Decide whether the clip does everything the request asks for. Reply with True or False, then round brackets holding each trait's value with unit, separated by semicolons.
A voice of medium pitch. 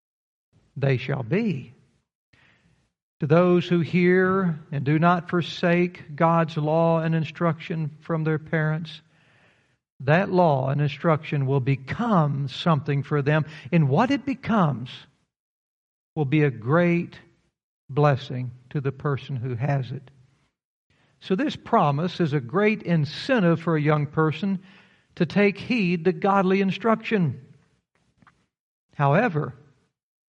True (155 Hz)